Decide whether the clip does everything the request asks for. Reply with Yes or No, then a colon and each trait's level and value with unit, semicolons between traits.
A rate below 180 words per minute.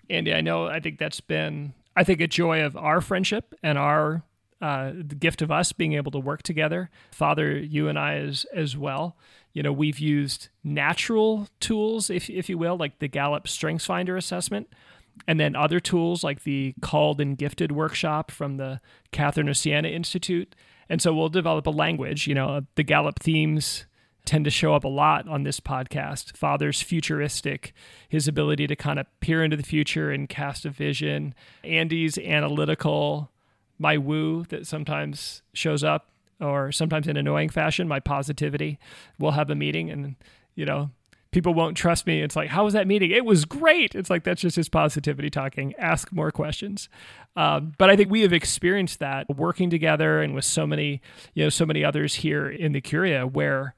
No: average, 185 wpm